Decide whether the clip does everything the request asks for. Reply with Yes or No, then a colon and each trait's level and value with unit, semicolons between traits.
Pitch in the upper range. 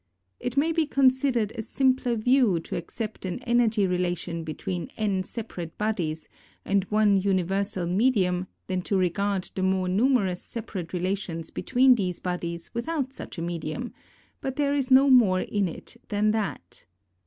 Yes: high, 200 Hz